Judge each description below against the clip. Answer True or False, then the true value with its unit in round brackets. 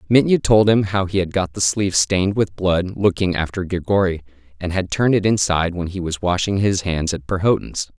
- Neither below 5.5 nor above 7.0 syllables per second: True (5.6 syllables/s)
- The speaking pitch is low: True (95 Hz)